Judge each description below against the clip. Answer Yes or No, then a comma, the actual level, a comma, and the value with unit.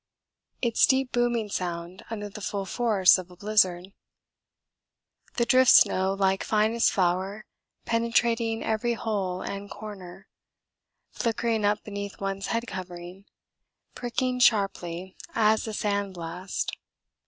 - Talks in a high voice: Yes, high, 205 Hz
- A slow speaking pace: Yes, slow, 120 wpm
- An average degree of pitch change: Yes, average, 3.5 semitones